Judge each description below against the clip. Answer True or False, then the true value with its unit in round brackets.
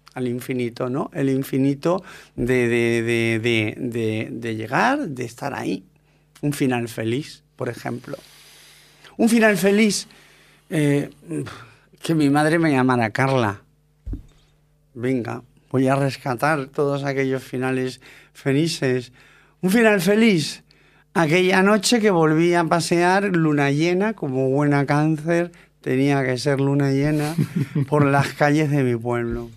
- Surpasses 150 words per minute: False (130 wpm)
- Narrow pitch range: False (4.1 semitones)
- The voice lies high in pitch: False (140 Hz)